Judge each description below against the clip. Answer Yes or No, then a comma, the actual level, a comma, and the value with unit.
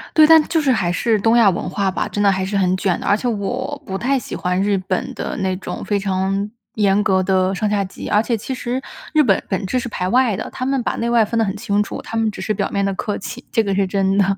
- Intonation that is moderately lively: Yes, average, 3.3 semitones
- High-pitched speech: Yes, high, 205 Hz